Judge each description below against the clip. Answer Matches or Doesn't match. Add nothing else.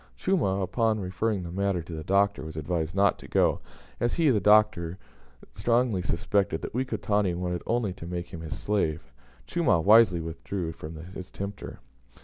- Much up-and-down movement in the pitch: Doesn't match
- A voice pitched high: Doesn't match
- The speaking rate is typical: Matches